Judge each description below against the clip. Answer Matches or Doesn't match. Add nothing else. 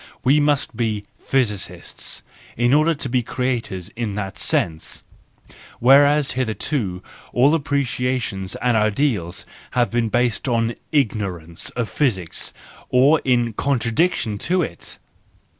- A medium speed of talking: Doesn't match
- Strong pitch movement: Doesn't match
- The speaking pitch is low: Matches